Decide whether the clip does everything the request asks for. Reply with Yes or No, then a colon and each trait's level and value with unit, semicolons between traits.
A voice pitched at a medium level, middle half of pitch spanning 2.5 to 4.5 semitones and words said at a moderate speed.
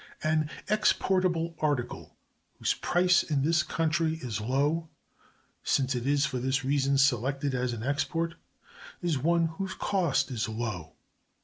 No: medium, 145 Hz; average, 4.2 semitones; slow, 125 wpm